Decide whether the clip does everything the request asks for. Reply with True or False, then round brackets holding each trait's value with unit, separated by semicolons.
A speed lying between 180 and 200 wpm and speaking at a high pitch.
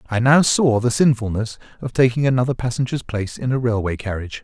False (190 wpm; 120 Hz)